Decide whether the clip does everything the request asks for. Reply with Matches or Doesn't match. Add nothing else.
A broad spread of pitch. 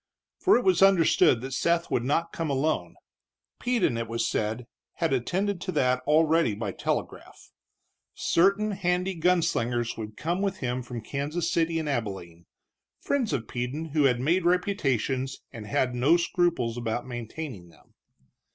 Matches